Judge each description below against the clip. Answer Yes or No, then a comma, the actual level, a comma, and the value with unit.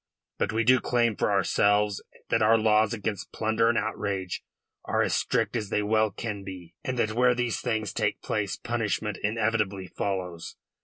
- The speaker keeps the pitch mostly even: Yes, narrow, 2.1 semitones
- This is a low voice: Yes, low, 110 Hz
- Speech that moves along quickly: No, average, 170 wpm